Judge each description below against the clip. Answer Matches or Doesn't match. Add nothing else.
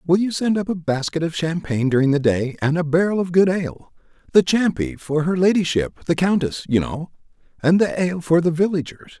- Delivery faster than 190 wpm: Matches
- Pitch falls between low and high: Matches